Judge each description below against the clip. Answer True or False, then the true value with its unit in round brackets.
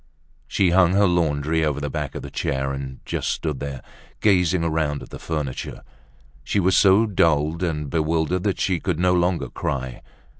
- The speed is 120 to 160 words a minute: False (180 wpm)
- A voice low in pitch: True (80 Hz)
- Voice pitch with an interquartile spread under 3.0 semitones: False (3.9 semitones)